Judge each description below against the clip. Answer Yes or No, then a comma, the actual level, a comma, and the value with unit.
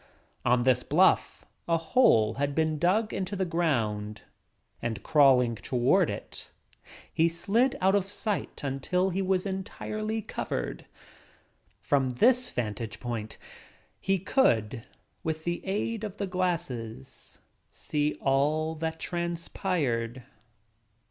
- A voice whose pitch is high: No, medium, 160 Hz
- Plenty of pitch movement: Yes, wide, 7.5 semitones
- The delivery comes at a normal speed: No, slow, 115 wpm